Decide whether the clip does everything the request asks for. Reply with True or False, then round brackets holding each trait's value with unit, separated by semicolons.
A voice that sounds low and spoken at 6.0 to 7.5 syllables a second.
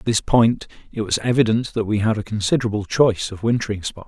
True (110 Hz; 6.2 syllables/s)